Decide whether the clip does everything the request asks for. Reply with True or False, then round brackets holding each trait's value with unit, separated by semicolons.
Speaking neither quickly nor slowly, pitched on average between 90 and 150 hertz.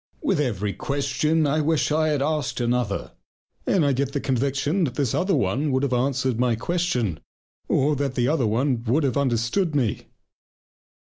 True (165 wpm; 135 Hz)